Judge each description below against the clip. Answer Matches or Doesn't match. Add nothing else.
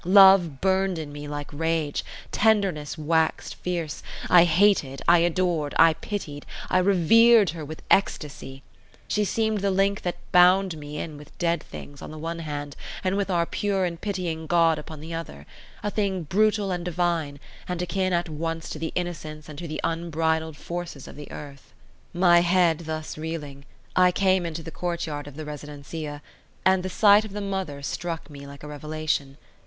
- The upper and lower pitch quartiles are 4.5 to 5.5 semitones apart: Doesn't match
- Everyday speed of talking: Matches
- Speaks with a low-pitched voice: Doesn't match